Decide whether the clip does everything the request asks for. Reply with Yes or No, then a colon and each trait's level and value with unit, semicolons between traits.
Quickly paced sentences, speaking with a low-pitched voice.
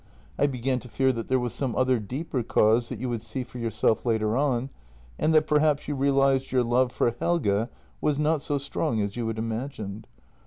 Yes: fast, 210 wpm; low, 125 Hz